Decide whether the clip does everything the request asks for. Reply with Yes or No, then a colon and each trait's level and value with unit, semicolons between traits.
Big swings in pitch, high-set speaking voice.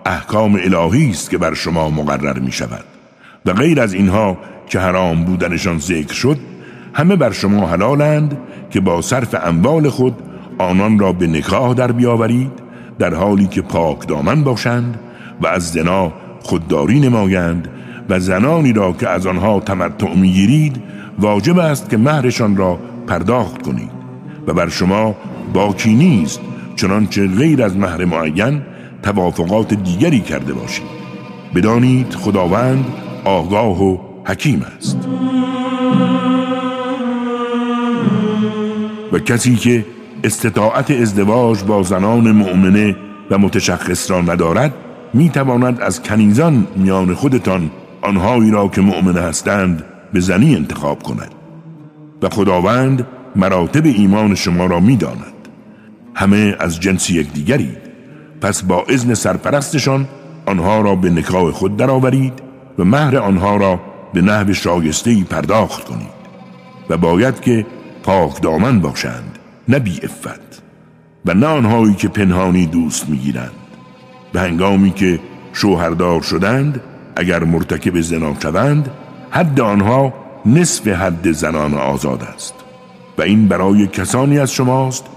No: wide, 5.9 semitones; low, 100 Hz